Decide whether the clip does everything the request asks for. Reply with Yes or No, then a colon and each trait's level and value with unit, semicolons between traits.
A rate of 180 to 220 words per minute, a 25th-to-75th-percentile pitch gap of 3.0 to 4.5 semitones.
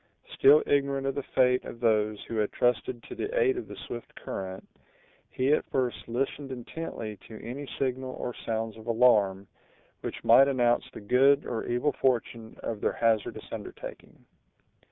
No: average, 165 wpm; average, 3.4 semitones